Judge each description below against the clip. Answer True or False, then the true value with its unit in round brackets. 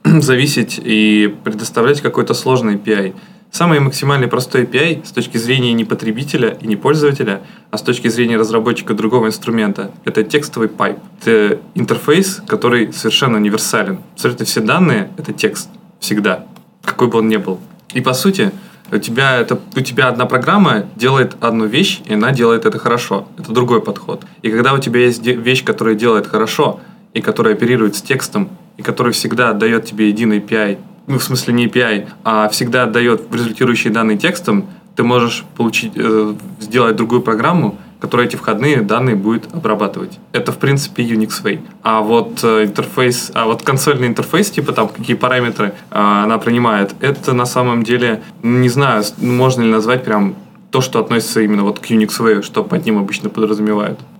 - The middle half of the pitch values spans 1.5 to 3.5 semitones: True (2.6 semitones)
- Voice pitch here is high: False (115 Hz)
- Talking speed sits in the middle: False (170 wpm)